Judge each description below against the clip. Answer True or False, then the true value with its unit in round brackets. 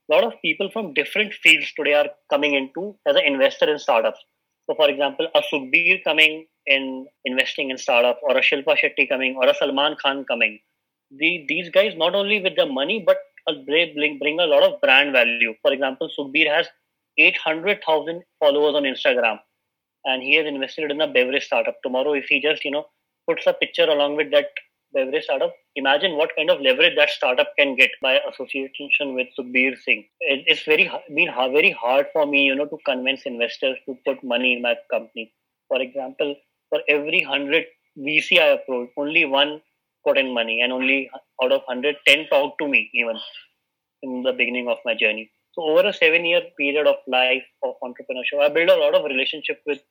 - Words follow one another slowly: False (190 wpm)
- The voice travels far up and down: True (6.7 semitones)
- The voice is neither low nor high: True (150 Hz)